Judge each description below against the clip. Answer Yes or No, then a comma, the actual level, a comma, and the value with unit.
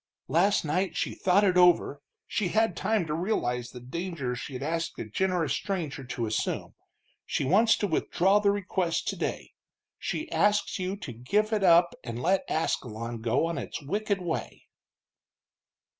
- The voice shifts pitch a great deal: Yes, wide, 6.3 semitones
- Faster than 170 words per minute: No, average, 160 wpm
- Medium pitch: Yes, medium, 175 Hz